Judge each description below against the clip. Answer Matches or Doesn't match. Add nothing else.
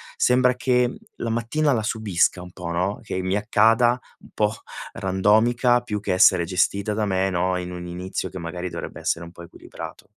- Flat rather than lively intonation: Doesn't match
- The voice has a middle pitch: Doesn't match